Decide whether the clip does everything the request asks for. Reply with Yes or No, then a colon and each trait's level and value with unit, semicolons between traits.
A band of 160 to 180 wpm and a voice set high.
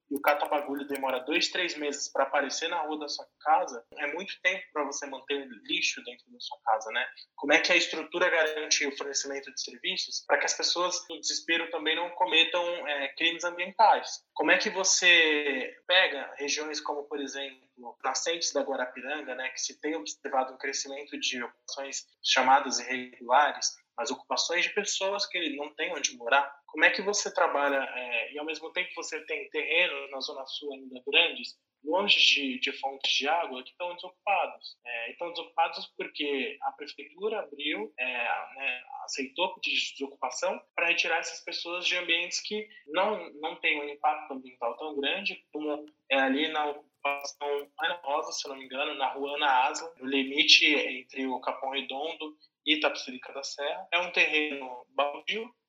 No: average, 175 wpm; medium, 150 Hz